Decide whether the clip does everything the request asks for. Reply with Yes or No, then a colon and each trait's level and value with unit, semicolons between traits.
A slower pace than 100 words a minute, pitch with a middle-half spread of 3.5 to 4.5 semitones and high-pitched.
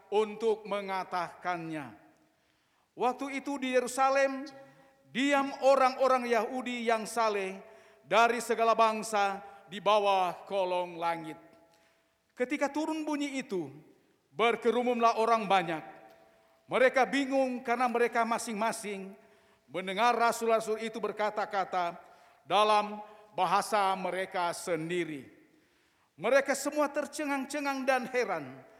No: average, 90 wpm; average, 5.1 semitones; high, 220 Hz